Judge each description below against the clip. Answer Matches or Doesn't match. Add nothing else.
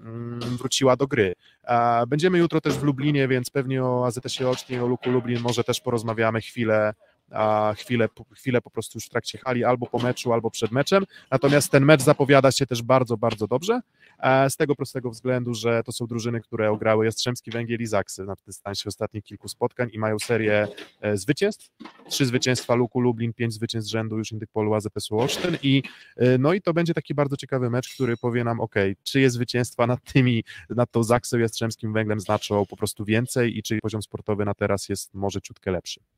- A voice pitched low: Matches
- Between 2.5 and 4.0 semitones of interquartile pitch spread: Matches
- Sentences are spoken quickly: Matches